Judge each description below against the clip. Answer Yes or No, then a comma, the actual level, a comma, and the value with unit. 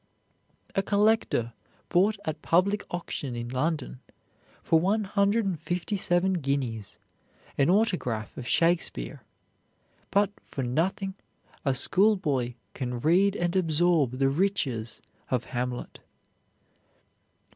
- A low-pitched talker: No, medium, 165 Hz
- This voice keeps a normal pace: No, slow, 110 wpm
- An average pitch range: No, wide, 7.3 semitones